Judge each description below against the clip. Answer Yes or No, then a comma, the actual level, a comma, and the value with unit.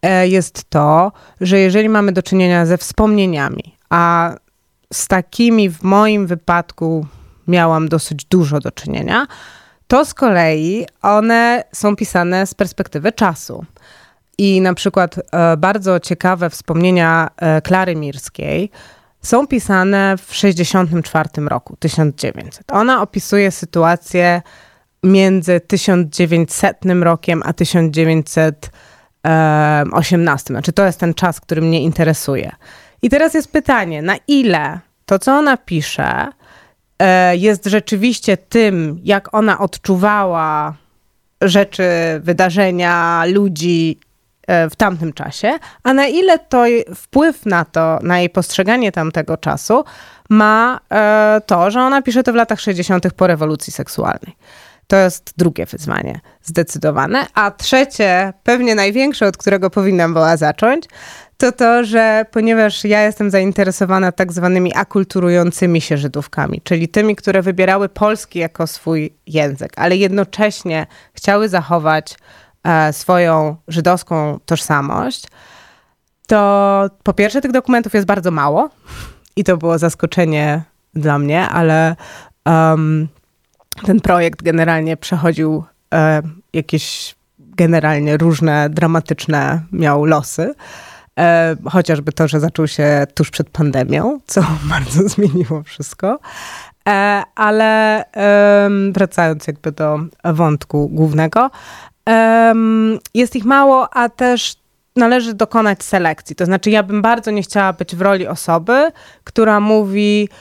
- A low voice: No, medium, 180 Hz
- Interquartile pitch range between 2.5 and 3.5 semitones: No, average, 4.3 semitones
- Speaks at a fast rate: No, average, 120 wpm